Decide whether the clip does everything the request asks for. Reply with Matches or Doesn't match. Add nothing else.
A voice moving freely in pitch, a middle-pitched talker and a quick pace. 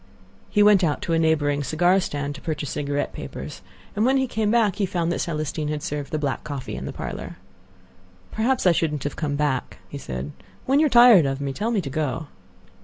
Matches